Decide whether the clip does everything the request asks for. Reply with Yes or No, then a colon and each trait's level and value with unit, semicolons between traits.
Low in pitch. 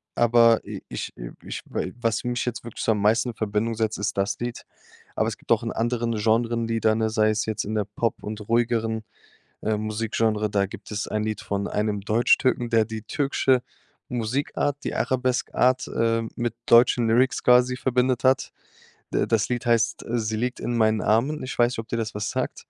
Yes: low, 115 Hz